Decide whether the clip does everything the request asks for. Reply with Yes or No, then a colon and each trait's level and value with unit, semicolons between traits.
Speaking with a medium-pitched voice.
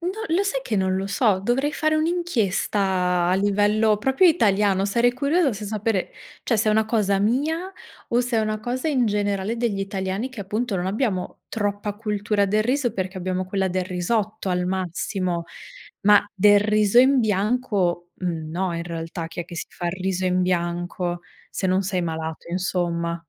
No: high, 200 Hz